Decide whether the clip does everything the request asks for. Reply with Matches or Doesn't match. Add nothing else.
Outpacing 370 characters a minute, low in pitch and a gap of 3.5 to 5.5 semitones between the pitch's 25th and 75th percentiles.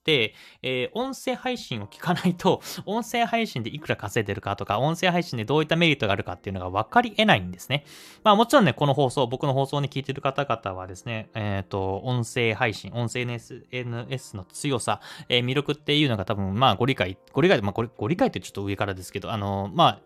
Doesn't match